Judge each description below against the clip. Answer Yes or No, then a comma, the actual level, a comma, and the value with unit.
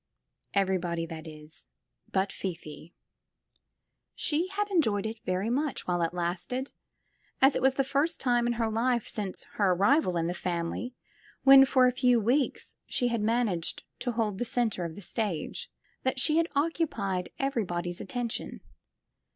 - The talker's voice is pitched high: Yes, high, 225 Hz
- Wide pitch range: Yes, wide, 6.4 semitones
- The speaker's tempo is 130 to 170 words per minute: Yes, average, 155 wpm